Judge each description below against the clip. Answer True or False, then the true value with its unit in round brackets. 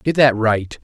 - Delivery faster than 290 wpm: False (215 wpm)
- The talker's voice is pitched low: True (120 Hz)